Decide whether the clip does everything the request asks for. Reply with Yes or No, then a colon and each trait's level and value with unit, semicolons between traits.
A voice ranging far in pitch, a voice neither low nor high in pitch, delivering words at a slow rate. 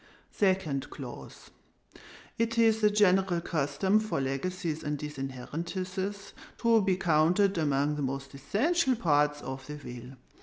Yes: wide, 6.1 semitones; medium, 165 Hz; slow, 125 wpm